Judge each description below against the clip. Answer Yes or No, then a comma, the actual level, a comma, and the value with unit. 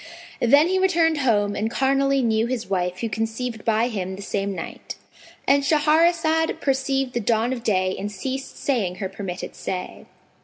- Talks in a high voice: Yes, high, 235 Hz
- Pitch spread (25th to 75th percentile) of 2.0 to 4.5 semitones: No, average, 5.3 semitones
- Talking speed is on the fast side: No, average, 160 wpm